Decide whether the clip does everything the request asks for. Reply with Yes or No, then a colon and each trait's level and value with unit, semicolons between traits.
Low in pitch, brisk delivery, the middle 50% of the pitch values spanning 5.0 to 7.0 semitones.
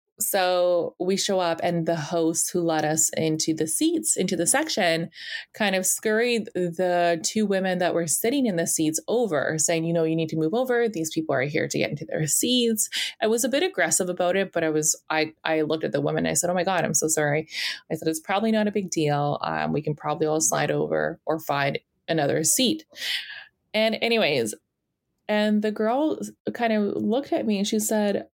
No: medium, 175 Hz; fast, 215 wpm; average, 5.3 semitones